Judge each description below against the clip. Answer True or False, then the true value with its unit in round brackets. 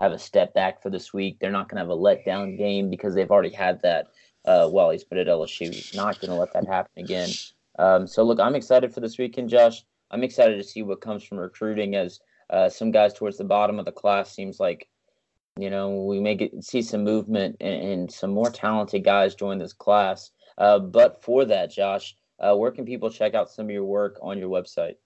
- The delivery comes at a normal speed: False (230 wpm)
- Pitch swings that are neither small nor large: False (2.2 semitones)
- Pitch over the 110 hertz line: False (105 Hz)